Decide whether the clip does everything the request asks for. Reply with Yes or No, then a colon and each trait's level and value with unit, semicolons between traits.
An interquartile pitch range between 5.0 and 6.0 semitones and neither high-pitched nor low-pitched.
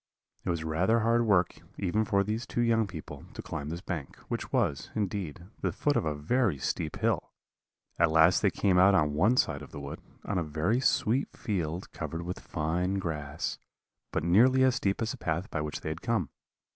No: wide, 5.5 semitones; very low, 90 Hz